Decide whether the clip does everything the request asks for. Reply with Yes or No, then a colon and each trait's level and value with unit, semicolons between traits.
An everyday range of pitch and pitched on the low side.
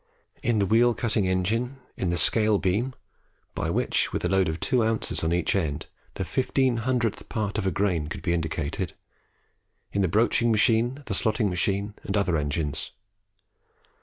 Yes: average, 4.4 semitones; low, 100 Hz